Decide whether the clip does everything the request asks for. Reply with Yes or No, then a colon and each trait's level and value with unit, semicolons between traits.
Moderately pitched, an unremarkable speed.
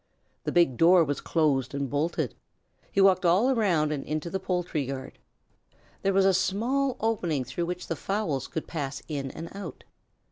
Yes: medium, 170 Hz; average, 175 wpm